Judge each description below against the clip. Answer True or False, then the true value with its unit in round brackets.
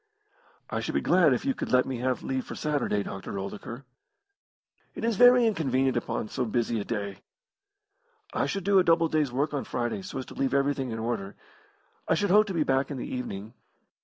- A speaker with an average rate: False (210 wpm)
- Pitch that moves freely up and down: True (5.8 semitones)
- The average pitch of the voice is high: False (135 Hz)